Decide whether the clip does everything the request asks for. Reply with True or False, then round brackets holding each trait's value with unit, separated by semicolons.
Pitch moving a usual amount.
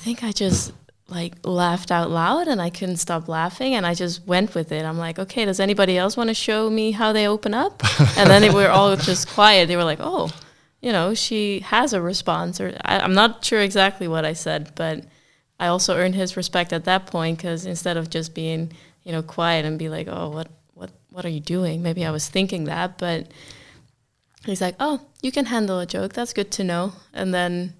True (3.3 semitones)